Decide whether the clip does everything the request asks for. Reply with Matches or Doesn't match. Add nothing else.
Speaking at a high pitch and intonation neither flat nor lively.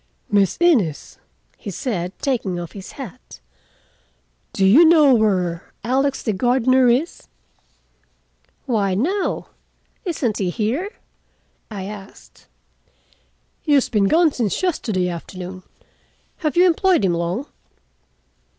Doesn't match